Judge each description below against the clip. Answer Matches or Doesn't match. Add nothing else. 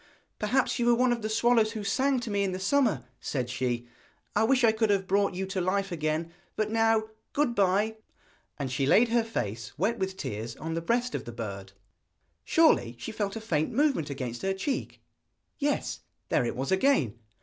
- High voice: Matches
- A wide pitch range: Matches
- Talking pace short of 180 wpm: Doesn't match